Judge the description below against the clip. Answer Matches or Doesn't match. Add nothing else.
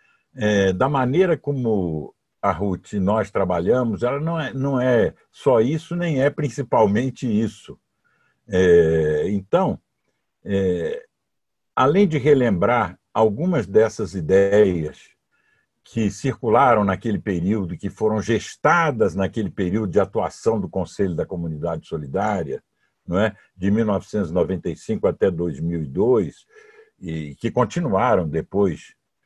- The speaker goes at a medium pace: Doesn't match